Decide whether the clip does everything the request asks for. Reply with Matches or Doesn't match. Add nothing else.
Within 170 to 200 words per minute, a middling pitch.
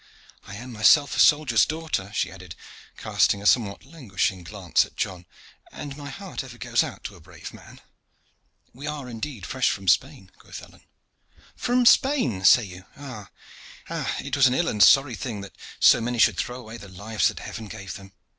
Doesn't match